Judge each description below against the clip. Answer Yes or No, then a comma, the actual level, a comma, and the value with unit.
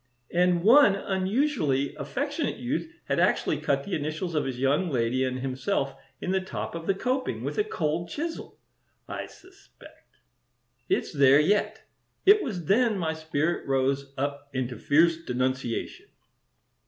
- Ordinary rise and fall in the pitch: No, wide, 7.1 semitones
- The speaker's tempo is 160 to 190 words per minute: No, average, 145 wpm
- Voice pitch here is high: No, medium, 165 Hz